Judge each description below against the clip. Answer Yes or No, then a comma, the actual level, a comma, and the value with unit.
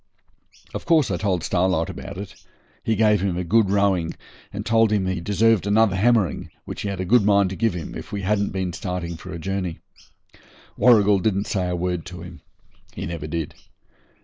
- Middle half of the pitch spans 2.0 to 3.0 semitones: Yes, average, 2.7 semitones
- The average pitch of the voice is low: Yes, very low, 95 Hz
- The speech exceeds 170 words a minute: Yes, average, 200 wpm